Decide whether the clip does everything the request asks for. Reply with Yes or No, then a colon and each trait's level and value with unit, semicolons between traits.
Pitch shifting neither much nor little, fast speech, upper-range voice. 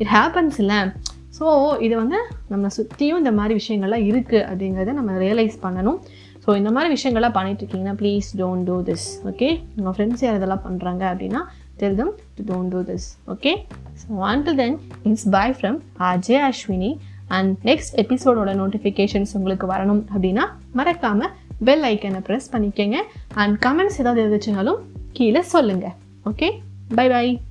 Yes: average, 4.5 semitones; fast, 140 wpm; high, 210 Hz